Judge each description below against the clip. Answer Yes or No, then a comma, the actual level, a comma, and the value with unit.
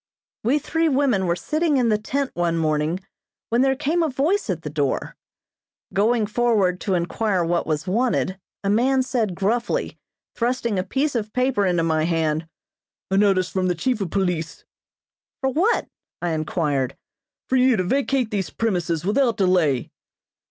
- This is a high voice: Yes, high, 205 Hz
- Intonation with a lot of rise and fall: Yes, wide, 6.8 semitones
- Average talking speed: Yes, average, 165 wpm